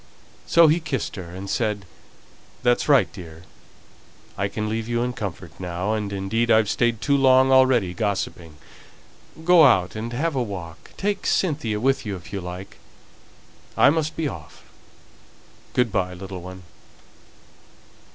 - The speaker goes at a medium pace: Yes, average, 150 wpm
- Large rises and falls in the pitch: Yes, wide, 5.8 semitones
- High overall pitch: No, low, 110 Hz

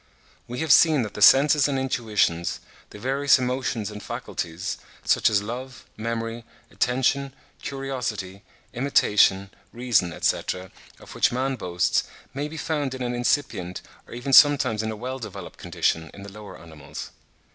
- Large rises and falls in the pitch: No, average, 4.6 semitones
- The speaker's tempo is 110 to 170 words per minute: Yes, average, 150 wpm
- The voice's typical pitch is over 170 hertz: No, low, 120 Hz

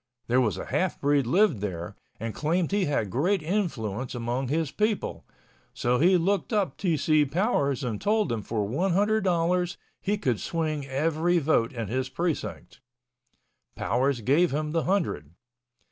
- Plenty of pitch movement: Yes, wide, 6.5 semitones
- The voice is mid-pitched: Yes, medium, 150 Hz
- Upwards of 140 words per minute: Yes, average, 160 wpm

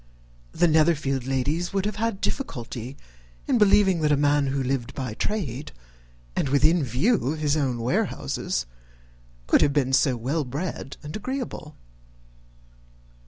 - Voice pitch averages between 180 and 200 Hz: No, medium, 145 Hz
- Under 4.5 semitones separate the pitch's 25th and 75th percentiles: No, average, 4.8 semitones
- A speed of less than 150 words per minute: Yes, average, 140 wpm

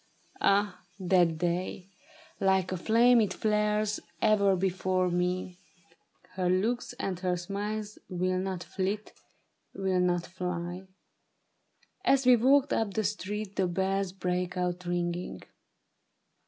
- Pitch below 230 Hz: Yes, high, 190 Hz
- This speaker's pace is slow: Yes, slow, 120 wpm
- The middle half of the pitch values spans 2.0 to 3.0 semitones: Yes, narrow, 2.6 semitones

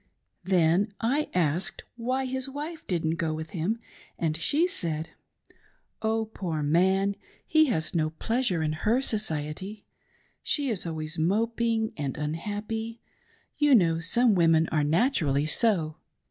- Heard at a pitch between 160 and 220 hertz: Yes, high, 190 Hz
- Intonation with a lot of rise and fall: Yes, wide, 6.3 semitones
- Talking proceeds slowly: Yes, slow, 130 wpm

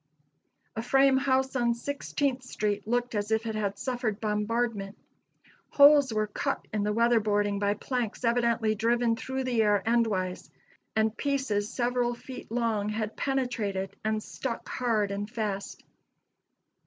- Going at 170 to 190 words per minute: No, average, 140 wpm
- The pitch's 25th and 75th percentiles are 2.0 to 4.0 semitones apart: Yes, average, 2.9 semitones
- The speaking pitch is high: Yes, high, 225 Hz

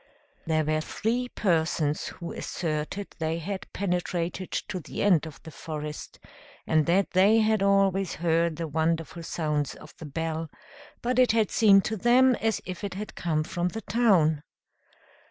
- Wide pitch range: No, average, 4.1 semitones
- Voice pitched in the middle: Yes, medium, 175 Hz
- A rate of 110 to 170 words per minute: Yes, average, 160 wpm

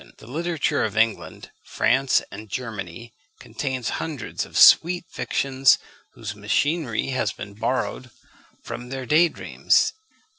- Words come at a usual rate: No, slow, 120 wpm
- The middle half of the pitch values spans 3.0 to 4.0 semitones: No, average, 4.6 semitones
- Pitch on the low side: Yes, low, 130 Hz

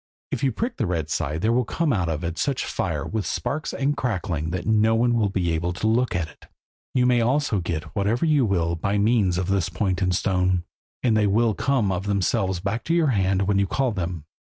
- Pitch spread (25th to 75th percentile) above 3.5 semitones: Yes, average, 4.9 semitones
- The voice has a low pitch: Yes, low, 100 Hz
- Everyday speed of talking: No, fast, 235 wpm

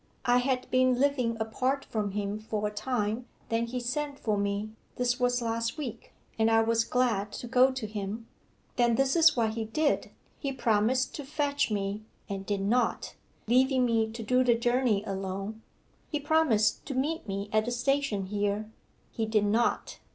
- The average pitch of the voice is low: No, high, 230 Hz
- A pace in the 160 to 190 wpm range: Yes, average, 180 wpm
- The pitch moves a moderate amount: Yes, average, 3.3 semitones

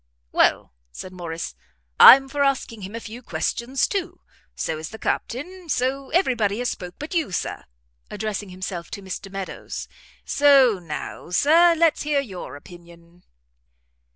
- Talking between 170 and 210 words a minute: No, average, 150 wpm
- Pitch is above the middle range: Yes, high, 225 Hz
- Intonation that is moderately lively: No, wide, 7.7 semitones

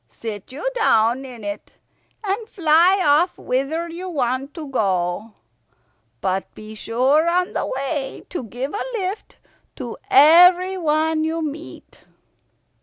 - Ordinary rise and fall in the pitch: No, wide, 6.1 semitones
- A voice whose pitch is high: Yes, very high, 300 Hz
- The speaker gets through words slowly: Yes, slow, 125 wpm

